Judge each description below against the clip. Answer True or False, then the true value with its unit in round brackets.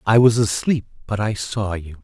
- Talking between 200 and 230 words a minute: True (205 wpm)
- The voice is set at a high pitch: False (105 Hz)